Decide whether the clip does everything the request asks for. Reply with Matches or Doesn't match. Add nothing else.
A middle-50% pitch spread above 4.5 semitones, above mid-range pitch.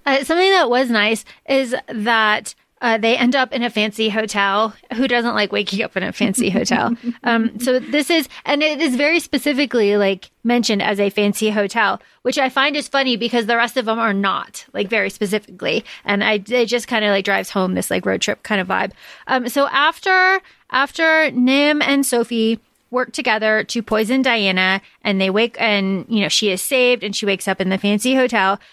Doesn't match